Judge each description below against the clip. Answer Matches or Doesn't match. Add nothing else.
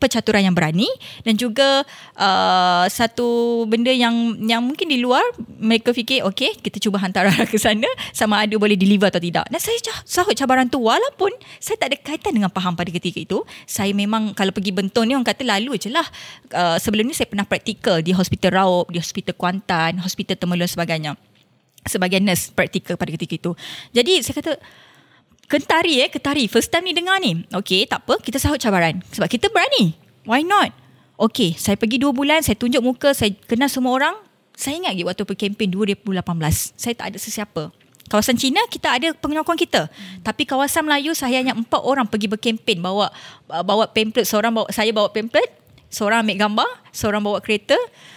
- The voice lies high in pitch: Matches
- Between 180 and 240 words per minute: Matches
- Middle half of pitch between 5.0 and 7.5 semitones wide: Matches